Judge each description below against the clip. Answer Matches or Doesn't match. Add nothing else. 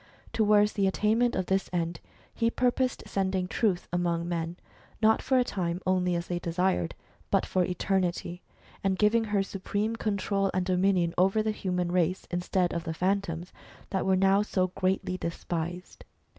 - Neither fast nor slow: Matches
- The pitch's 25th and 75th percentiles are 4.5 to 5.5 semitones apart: Doesn't match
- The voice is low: Doesn't match